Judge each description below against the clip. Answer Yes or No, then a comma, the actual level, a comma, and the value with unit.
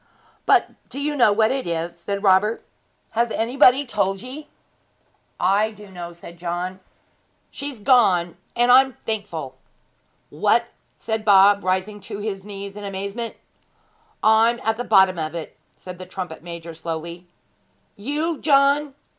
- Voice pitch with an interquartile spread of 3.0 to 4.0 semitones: No, average, 4.8 semitones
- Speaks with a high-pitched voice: Yes, high, 200 Hz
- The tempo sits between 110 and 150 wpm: Yes, average, 145 wpm